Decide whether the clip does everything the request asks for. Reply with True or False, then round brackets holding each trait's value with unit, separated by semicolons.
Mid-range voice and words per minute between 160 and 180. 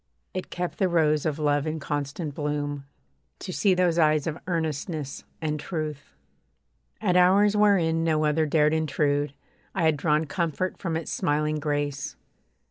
False (155 Hz; 150 wpm)